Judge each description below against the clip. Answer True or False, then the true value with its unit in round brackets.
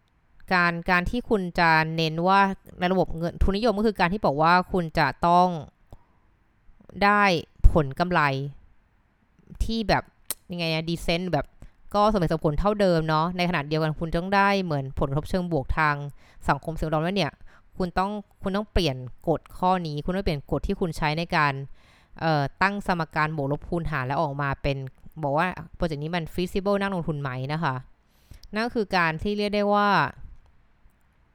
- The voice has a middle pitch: True (170 Hz)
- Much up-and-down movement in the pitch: False (4.0 semitones)